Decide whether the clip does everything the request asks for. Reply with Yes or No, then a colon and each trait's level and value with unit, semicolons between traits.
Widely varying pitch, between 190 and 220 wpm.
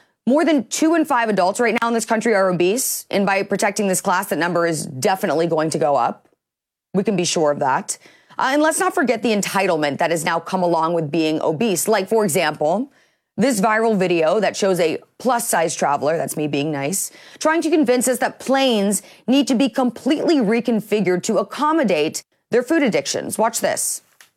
Yes: wide, 6.9 semitones; average, 200 wpm